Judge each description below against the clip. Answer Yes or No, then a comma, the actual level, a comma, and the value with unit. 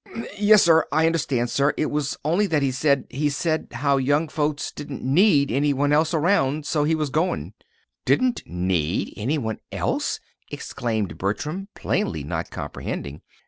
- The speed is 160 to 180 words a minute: Yes, average, 165 wpm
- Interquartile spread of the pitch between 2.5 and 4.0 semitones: Yes, average, 3.4 semitones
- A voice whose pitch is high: No, medium, 145 Hz